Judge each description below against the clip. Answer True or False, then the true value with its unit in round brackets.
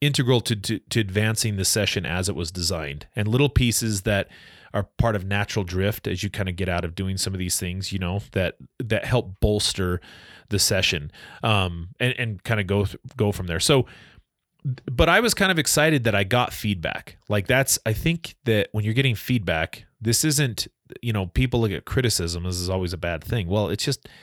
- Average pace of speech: False (215 wpm)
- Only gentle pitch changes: False (4.4 semitones)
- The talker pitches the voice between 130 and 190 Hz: False (105 Hz)